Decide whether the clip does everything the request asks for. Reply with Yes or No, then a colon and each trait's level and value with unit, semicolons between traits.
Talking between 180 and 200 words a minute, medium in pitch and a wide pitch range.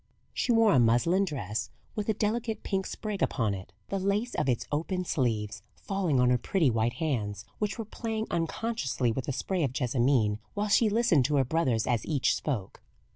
Yes: average, 190 wpm; medium, 150 Hz; wide, 9.0 semitones